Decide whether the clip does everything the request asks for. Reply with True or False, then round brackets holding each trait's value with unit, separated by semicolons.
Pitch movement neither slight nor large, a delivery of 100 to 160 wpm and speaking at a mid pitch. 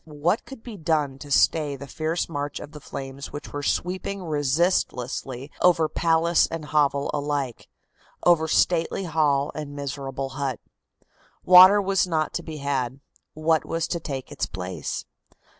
True (3.1 semitones; 150 wpm; 150 Hz)